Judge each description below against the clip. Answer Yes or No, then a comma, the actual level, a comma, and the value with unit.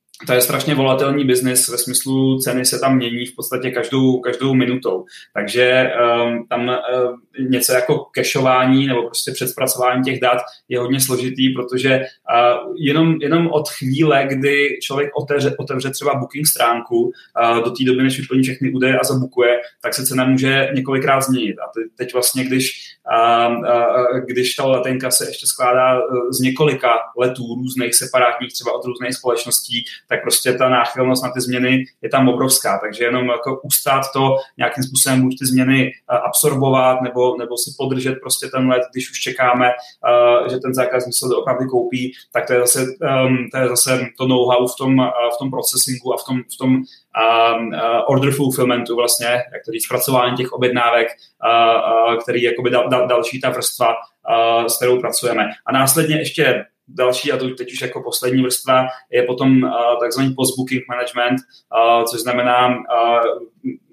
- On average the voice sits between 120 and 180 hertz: Yes, low, 125 Hz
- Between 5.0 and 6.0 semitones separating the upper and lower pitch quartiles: No, narrow, 1.3 semitones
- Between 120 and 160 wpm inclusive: No, fast, 170 wpm